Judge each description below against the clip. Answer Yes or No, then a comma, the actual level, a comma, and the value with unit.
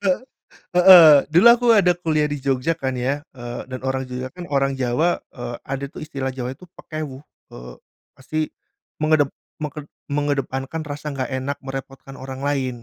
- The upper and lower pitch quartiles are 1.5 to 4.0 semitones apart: Yes, average, 2.9 semitones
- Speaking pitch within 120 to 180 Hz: Yes, medium, 140 Hz